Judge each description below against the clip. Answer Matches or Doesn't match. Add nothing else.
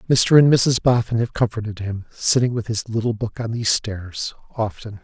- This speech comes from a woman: Doesn't match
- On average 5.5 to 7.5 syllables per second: Doesn't match